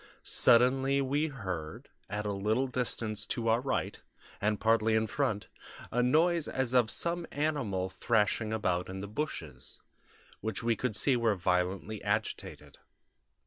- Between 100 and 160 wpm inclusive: Yes, average, 145 wpm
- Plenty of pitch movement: No, average, 4.4 semitones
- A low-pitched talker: Yes, low, 110 Hz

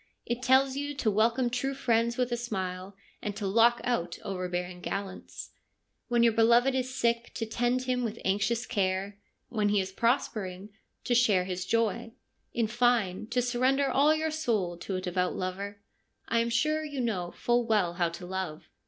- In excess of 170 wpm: Yes, average, 180 wpm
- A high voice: Yes, high, 230 Hz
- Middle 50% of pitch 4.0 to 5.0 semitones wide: Yes, average, 4.4 semitones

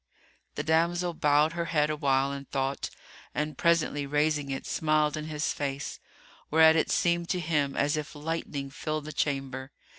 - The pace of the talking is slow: No, average, 160 wpm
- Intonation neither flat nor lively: No, narrow, 2.2 semitones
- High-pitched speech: No, medium, 150 Hz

